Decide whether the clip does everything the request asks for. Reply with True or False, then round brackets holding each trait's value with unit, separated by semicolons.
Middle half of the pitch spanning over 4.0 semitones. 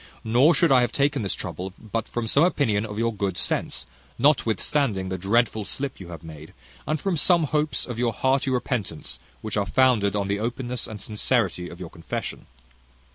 True (5.1 semitones)